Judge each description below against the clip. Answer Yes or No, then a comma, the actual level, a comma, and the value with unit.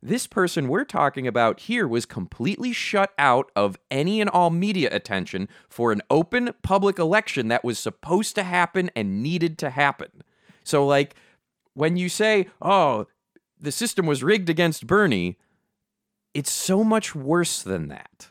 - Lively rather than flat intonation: Yes, wide, 6.7 semitones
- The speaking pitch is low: No, medium, 170 Hz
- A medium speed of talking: Yes, average, 155 wpm